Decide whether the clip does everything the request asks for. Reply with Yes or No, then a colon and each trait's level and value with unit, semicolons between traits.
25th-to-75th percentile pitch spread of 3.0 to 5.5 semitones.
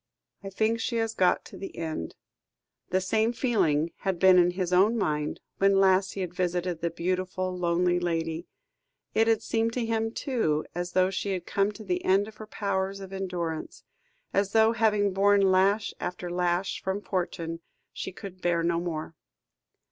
No: narrow, 2.5 semitones